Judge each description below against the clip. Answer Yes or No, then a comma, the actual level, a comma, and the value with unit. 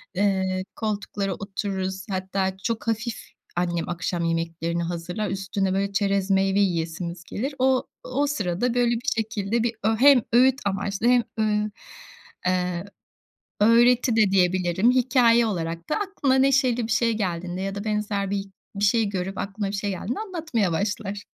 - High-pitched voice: Yes, high, 200 Hz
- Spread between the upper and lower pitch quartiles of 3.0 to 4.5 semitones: Yes, average, 3.8 semitones